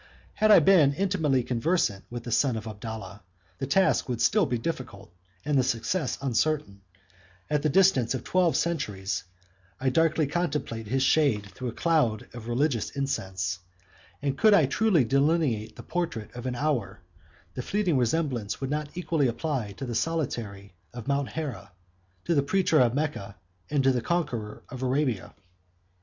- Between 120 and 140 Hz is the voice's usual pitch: Yes, low, 135 Hz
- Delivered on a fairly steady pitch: No, wide, 5.5 semitones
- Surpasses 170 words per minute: No, average, 165 wpm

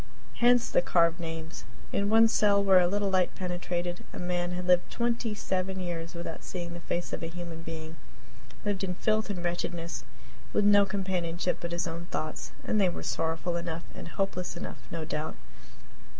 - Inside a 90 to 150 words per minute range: No, average, 180 wpm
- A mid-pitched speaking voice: Yes, medium, 175 Hz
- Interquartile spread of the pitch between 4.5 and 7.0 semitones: No, narrow, 2.4 semitones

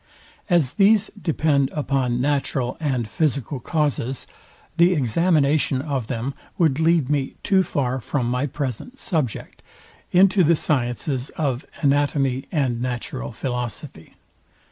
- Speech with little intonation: No, average, 3.9 semitones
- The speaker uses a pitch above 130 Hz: Yes, medium, 140 Hz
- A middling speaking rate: No, slow, 120 wpm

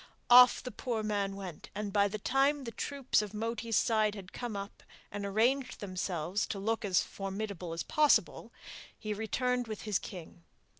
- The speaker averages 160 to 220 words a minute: Yes, average, 170 wpm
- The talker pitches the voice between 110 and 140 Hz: No, high, 210 Hz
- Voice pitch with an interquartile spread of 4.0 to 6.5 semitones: No, average, 3.2 semitones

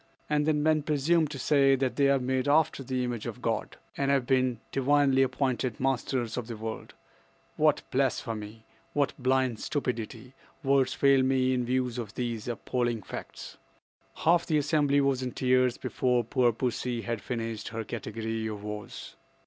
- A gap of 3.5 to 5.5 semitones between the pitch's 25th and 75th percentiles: No, average, 2.9 semitones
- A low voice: Yes, low, 130 Hz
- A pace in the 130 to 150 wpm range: No, average, 165 wpm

